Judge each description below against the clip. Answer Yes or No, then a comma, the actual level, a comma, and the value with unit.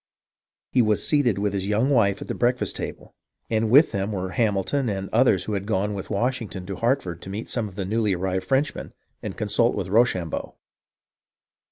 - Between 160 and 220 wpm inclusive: Yes, average, 190 wpm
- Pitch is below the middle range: Yes, low, 105 Hz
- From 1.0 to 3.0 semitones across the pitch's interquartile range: No, average, 3.8 semitones